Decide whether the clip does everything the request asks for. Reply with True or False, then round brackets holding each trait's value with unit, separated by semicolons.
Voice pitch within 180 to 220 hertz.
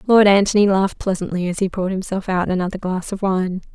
True (190 Hz)